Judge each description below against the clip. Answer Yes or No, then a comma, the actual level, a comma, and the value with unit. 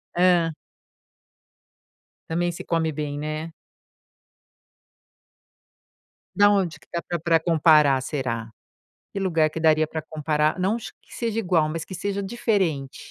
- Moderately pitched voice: Yes, medium, 165 Hz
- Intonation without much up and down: No, average, 3.1 semitones